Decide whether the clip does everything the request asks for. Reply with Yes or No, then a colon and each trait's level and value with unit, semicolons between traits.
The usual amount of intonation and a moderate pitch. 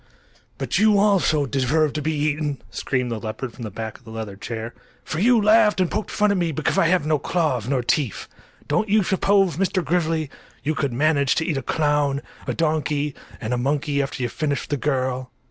Yes: average, 4.5 semitones; medium, 150 Hz